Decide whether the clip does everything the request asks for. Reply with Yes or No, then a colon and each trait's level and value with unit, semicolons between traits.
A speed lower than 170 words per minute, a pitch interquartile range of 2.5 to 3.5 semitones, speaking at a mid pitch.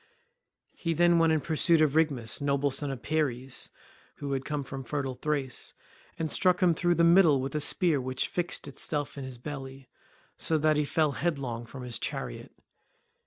No: average, 180 wpm; average, 3.2 semitones; medium, 145 Hz